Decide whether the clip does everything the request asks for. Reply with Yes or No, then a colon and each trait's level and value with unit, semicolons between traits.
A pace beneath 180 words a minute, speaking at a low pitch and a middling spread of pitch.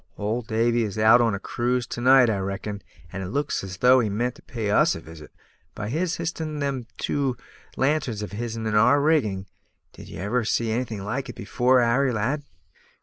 No: fast, 205 wpm; low, 120 Hz; average, 3.7 semitones